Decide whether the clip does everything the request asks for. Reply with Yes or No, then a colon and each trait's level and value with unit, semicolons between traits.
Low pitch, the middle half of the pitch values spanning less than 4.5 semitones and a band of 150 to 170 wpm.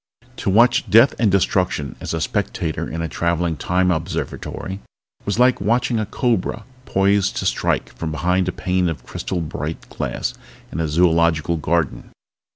Yes: very low, 90 Hz; average, 3.6 semitones; average, 160 wpm